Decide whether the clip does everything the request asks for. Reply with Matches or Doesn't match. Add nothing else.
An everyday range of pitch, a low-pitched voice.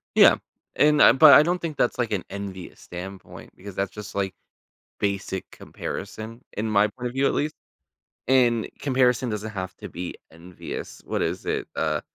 Matches